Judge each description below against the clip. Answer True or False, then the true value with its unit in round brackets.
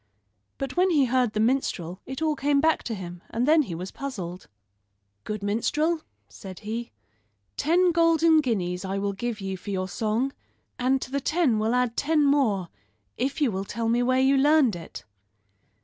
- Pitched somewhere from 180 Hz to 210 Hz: False (245 Hz)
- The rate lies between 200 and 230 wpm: False (180 wpm)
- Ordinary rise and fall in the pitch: False (6.2 semitones)